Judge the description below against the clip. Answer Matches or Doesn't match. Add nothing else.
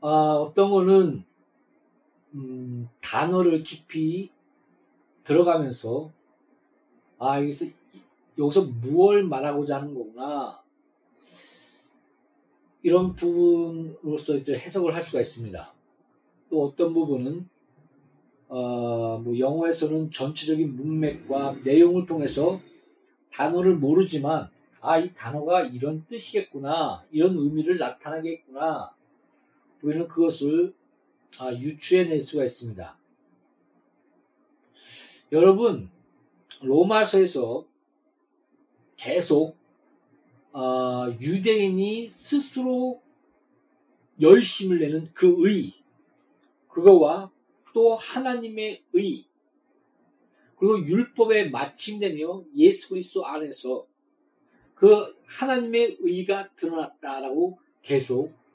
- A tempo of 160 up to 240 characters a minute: Matches